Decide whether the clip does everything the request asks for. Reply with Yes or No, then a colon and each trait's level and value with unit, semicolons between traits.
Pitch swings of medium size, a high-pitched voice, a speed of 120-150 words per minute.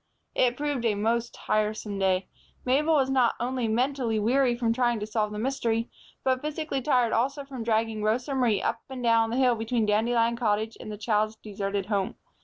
No: average, 3.0 semitones; high, 230 Hz; average, 190 wpm